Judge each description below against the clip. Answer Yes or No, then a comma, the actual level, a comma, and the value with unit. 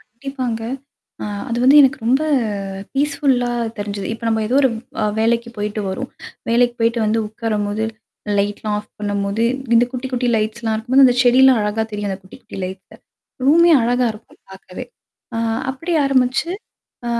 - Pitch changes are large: No, average, 3.4 semitones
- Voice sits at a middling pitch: No, high, 230 Hz